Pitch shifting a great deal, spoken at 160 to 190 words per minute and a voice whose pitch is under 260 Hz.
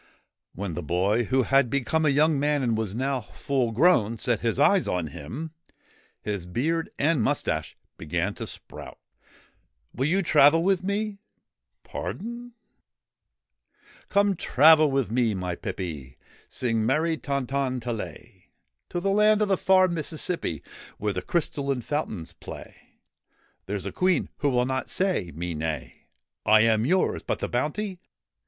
Yes: wide, 7.5 semitones; average, 165 wpm; low, 135 Hz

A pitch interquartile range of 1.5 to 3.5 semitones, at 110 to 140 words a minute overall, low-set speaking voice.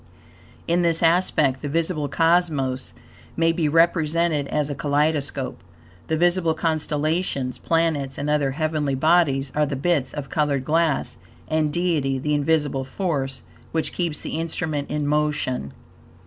No: average, 2.8 semitones; slow, 135 wpm; medium, 150 Hz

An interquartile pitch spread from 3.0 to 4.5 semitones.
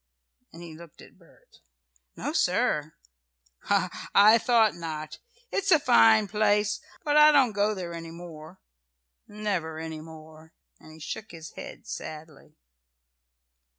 No: average, 5.1 semitones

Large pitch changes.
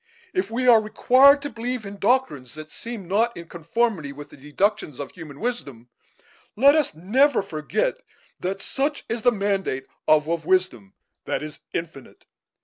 Yes: wide, 7.9 semitones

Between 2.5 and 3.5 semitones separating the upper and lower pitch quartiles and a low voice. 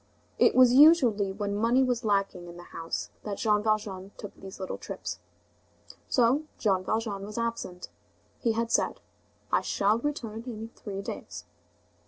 No: average, 2.9 semitones; high, 215 Hz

